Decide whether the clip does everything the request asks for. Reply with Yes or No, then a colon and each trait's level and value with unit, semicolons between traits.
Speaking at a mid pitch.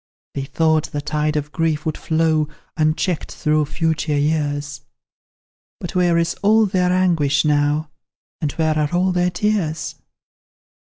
Yes: medium, 155 Hz